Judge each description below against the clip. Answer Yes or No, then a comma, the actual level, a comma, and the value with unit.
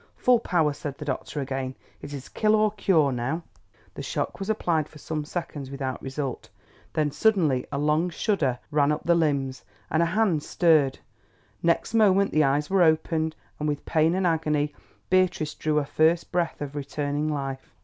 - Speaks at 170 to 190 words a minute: Yes, average, 180 wpm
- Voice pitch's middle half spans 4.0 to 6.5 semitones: No, average, 3.3 semitones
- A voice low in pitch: No, medium, 155 Hz